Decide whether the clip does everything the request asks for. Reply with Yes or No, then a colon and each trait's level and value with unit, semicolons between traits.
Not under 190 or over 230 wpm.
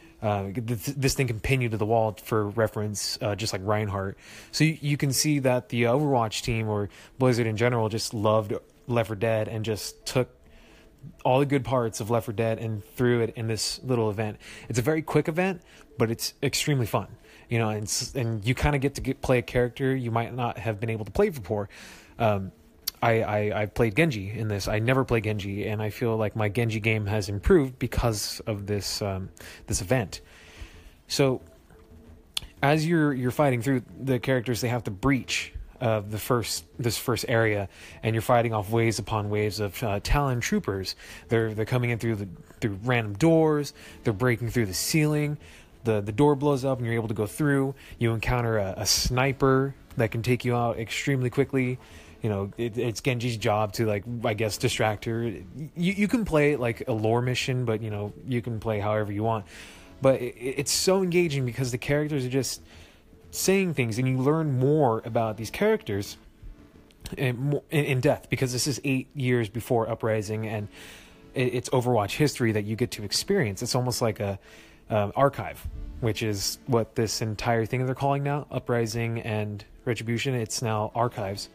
Yes: average, 195 wpm